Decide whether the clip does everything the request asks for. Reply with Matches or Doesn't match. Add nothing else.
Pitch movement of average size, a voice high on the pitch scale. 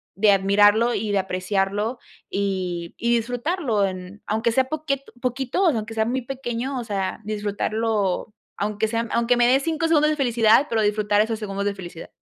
Matches